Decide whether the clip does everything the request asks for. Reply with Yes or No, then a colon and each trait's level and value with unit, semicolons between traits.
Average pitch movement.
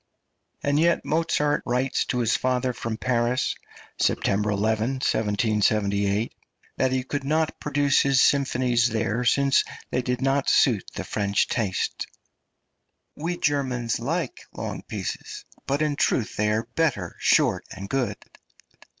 Yes: average, 4.3 semitones